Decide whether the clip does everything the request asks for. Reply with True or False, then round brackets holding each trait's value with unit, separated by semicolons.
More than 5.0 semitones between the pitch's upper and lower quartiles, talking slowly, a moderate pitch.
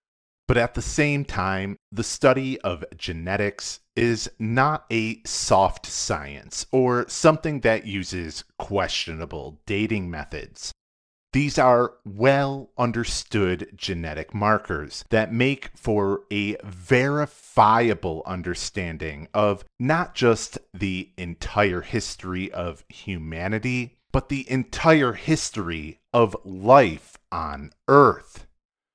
False (5.4 semitones; 100 wpm; 110 Hz)